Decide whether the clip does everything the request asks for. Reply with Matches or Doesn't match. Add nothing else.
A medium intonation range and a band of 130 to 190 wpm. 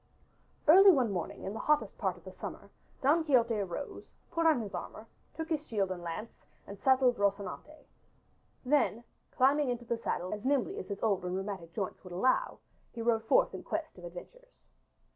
Doesn't match